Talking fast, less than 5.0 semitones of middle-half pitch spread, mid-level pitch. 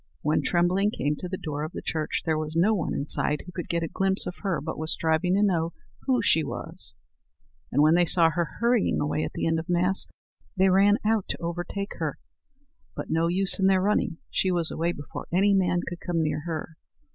Yes: fast, 220 wpm; average, 3.0 semitones; medium, 175 Hz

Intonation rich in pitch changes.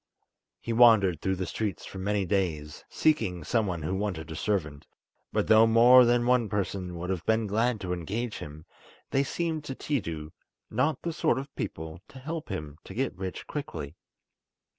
Yes: wide, 5.8 semitones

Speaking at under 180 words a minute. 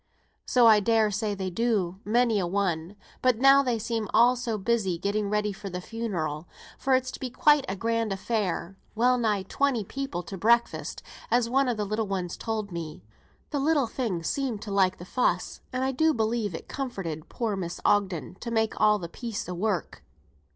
No: average, 195 wpm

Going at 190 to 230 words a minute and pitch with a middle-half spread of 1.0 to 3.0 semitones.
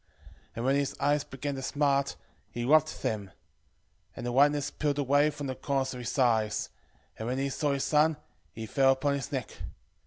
Yes: fast, 205 wpm; narrow, 2.5 semitones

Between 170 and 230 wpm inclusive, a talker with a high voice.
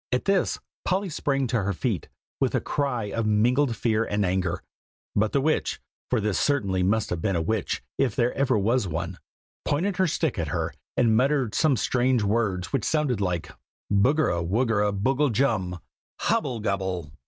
No: average, 175 wpm; low, 110 Hz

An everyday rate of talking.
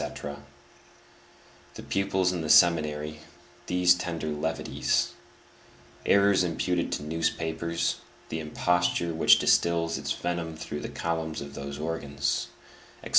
No: slow, 120 wpm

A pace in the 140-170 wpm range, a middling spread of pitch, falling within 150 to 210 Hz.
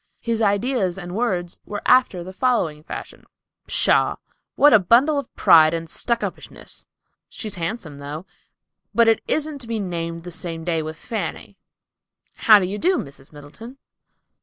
No: average, 160 wpm; wide, 5.9 semitones; high, 190 Hz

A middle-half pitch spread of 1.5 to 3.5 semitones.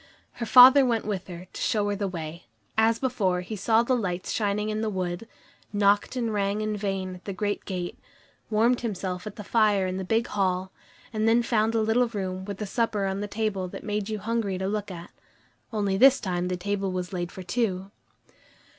Yes: average, 2.9 semitones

